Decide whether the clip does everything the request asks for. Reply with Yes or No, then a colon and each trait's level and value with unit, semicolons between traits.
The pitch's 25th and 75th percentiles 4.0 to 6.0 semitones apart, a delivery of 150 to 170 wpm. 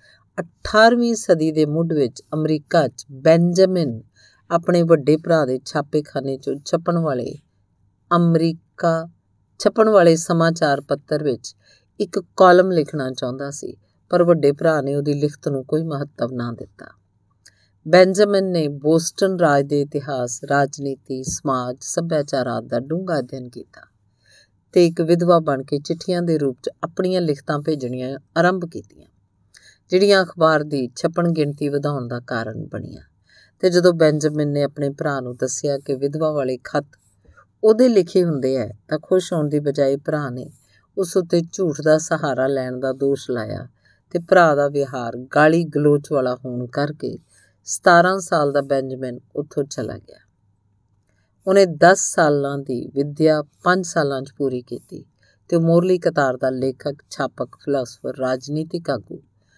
No: average, 4.4 semitones; average, 140 wpm